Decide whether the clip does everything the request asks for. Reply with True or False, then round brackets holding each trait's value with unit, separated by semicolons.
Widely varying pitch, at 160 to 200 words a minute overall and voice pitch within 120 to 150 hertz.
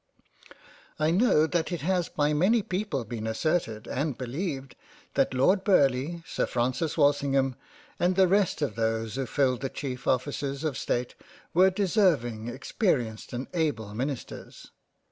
False (5.7 semitones; 145 wpm; 140 Hz)